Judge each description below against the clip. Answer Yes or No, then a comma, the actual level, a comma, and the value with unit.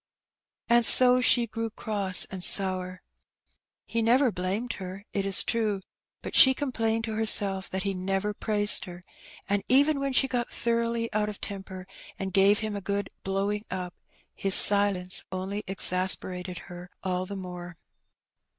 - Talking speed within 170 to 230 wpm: No, average, 155 wpm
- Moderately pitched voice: No, high, 200 Hz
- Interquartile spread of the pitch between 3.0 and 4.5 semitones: Yes, average, 3.4 semitones